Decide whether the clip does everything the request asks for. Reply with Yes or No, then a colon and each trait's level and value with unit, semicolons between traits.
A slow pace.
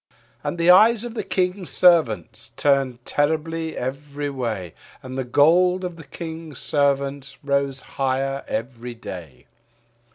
Yes: slow, 130 wpm